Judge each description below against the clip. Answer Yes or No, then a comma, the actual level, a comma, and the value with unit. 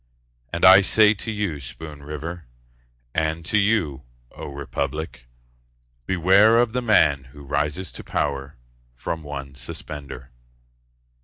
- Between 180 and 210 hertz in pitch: No, very low, 75 Hz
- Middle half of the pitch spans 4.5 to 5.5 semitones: Yes, average, 5.1 semitones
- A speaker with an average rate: No, slow, 125 wpm